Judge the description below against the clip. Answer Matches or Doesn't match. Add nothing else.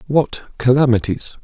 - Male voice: Matches